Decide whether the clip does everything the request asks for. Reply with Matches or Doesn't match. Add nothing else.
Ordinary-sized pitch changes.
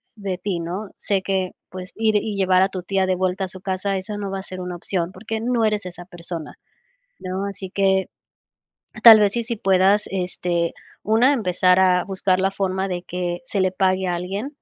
Doesn't match